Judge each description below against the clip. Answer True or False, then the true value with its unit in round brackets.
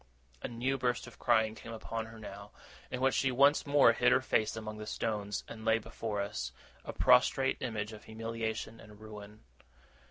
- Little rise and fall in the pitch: True (1.9 semitones)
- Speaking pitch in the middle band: False (110 Hz)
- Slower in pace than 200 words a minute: True (185 wpm)